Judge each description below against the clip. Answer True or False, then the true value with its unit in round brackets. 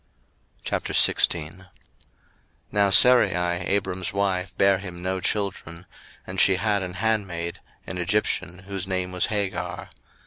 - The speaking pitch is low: True (95 Hz)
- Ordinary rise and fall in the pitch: False (1.9 semitones)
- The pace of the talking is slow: True (115 wpm)